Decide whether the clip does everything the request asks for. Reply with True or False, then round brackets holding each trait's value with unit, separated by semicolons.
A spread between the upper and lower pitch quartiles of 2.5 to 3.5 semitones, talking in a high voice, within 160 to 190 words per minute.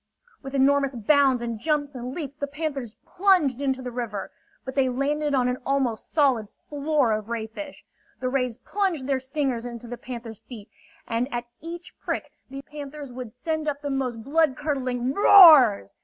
True (3.2 semitones; 265 Hz; 170 wpm)